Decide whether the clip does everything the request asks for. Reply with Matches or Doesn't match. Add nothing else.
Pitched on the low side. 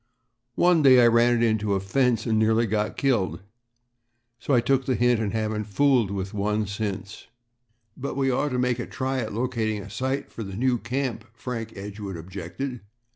Matches